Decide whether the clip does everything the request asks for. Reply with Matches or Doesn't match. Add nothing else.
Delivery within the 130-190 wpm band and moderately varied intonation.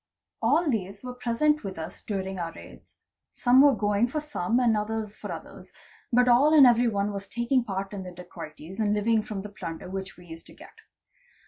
Doesn't match